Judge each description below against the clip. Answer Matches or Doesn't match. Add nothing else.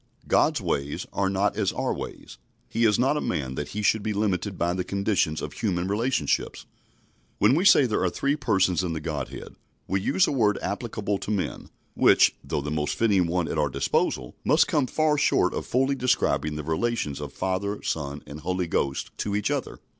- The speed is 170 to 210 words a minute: Matches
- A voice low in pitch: Matches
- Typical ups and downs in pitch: Doesn't match